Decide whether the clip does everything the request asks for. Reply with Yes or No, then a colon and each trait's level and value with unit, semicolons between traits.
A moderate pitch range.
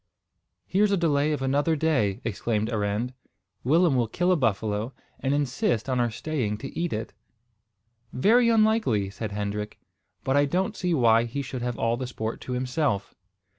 No: wide, 6.1 semitones